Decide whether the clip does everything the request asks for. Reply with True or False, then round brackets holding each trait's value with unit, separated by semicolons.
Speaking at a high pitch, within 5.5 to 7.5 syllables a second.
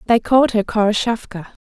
True (220 Hz; 6.0 syllables/s)